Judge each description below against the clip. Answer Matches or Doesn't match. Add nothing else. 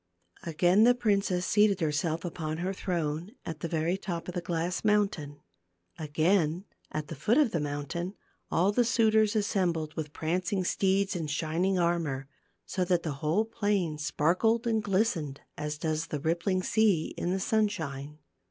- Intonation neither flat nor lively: Matches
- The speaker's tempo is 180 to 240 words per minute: Doesn't match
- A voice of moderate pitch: Matches